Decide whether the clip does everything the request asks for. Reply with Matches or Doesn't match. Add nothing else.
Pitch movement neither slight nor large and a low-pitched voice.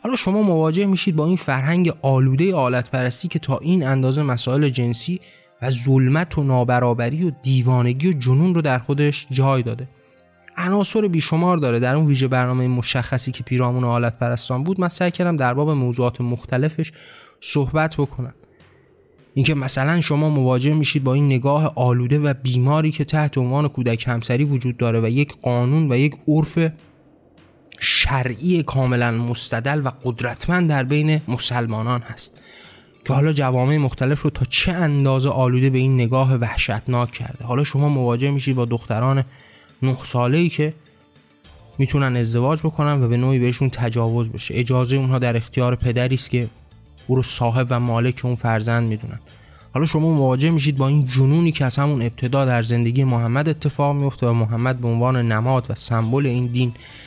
Matches